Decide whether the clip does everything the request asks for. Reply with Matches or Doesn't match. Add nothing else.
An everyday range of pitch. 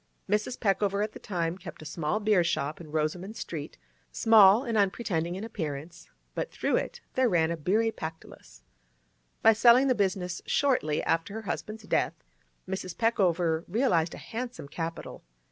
Matches